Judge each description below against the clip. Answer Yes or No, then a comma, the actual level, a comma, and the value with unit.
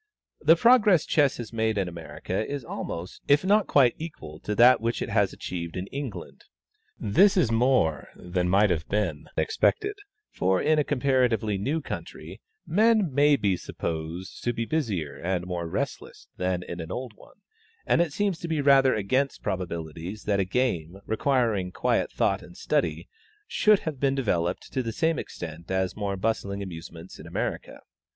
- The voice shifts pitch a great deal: Yes, wide, 7.9 semitones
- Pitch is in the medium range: No, low, 110 Hz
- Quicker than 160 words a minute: Yes, average, 170 wpm